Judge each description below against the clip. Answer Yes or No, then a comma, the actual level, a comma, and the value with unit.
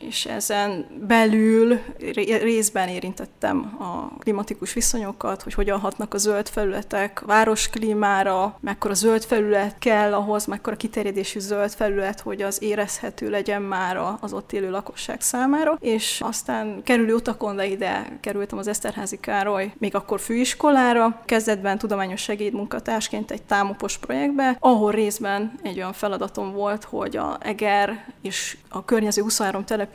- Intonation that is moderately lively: No, narrow, 2.1 semitones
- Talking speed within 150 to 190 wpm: No, average, 135 wpm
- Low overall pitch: No, high, 210 Hz